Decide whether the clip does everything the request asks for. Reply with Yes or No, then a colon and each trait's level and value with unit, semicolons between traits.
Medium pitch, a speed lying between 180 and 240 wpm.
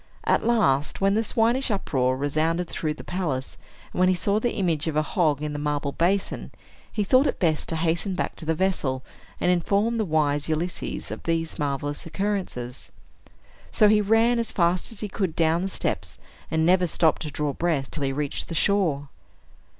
Yes: medium, 165 Hz; average, 195 wpm